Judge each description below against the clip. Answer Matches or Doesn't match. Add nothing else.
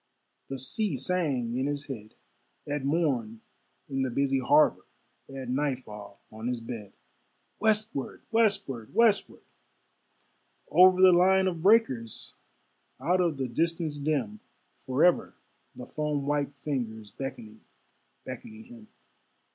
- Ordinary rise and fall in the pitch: Doesn't match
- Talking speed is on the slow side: Matches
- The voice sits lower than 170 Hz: Matches